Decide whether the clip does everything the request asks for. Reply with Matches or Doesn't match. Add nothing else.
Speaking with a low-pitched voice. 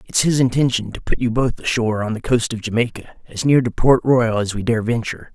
Matches